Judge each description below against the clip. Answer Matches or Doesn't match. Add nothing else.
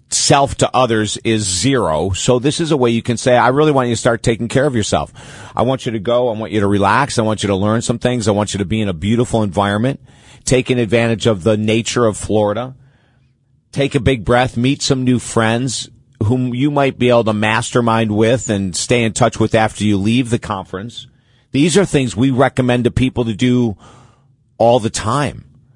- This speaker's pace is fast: Matches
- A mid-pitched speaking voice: Doesn't match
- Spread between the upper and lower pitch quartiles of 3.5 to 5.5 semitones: Doesn't match